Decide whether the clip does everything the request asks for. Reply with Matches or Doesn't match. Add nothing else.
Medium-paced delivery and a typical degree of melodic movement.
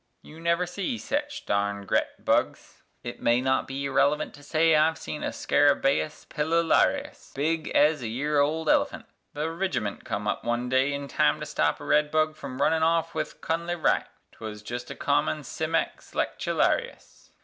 Matches